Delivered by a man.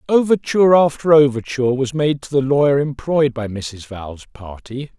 Yes: male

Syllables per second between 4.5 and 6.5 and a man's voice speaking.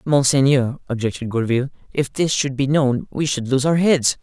Yes: 5.1 syllables/s; male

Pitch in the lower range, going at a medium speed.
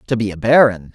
No: low, 105 Hz; fast, 255 wpm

